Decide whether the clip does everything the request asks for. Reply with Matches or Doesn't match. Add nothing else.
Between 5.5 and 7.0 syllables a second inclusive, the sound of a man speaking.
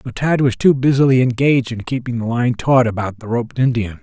Matches